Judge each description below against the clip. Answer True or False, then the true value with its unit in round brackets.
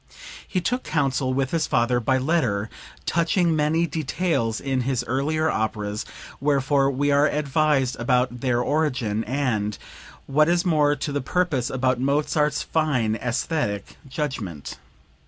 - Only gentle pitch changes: False (3.8 semitones)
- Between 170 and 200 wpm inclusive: False (135 wpm)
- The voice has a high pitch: False (135 Hz)